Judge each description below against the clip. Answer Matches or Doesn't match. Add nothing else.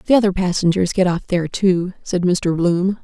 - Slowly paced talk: Doesn't match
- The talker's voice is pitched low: Doesn't match